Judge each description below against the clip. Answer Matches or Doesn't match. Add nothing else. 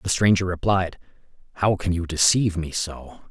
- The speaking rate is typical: Matches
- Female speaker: Doesn't match